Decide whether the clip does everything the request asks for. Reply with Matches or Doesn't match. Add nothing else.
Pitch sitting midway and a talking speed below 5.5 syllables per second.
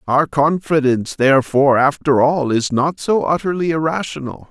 Matches